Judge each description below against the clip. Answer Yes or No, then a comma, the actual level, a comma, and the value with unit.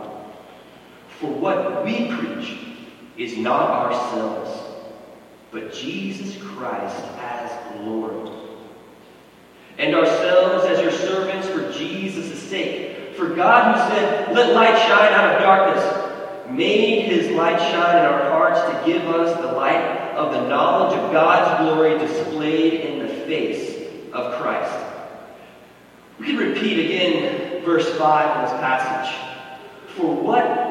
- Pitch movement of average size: No, wide, 6.8 semitones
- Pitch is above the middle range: No, medium, 165 Hz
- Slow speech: Yes, slow, 125 wpm